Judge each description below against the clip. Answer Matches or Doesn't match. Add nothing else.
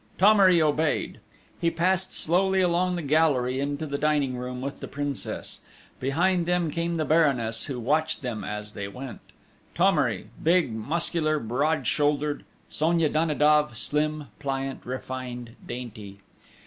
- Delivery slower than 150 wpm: Matches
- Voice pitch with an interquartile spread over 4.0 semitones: Matches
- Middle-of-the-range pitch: Matches